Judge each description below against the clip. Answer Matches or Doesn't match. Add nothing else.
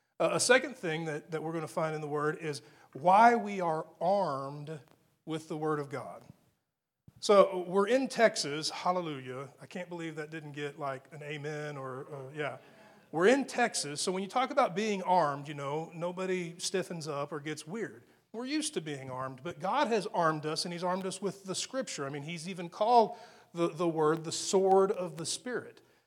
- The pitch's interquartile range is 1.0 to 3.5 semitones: Doesn't match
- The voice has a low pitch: Doesn't match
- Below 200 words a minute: Doesn't match